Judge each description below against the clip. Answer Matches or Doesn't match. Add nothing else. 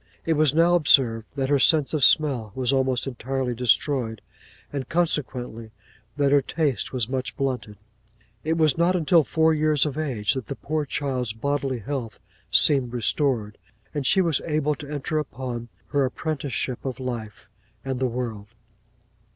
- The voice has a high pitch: Doesn't match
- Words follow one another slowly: Doesn't match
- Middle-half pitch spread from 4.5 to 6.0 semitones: Doesn't match